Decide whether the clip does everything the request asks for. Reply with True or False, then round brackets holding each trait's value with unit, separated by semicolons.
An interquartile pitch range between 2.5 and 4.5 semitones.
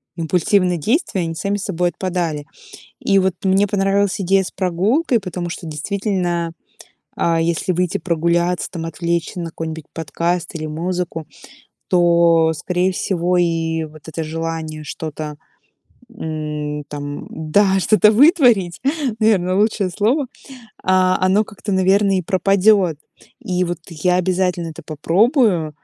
True (3.0 semitones)